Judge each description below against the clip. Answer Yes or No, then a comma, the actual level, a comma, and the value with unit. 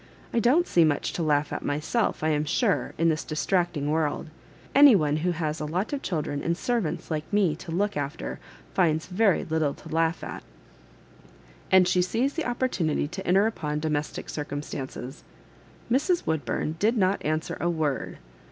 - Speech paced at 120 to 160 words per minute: No, average, 170 wpm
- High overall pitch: No, medium, 165 Hz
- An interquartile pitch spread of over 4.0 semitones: Yes, average, 4.7 semitones